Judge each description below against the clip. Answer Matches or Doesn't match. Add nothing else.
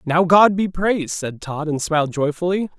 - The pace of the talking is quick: Doesn't match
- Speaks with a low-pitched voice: Doesn't match